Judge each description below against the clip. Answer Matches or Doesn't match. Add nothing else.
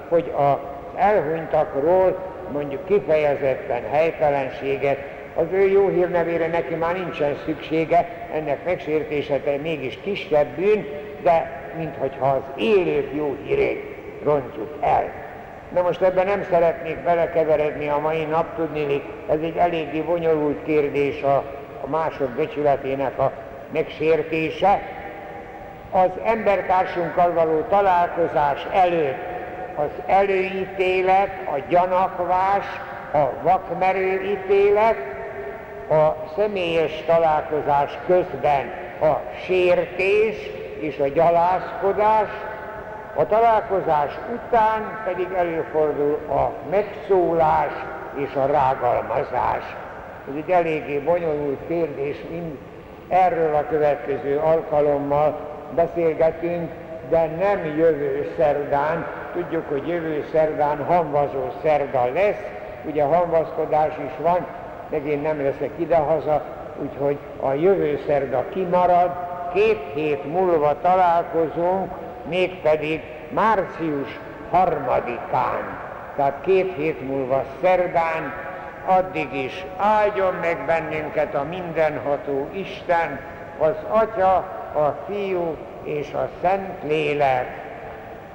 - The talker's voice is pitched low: Doesn't match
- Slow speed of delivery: Matches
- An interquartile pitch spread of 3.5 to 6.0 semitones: Matches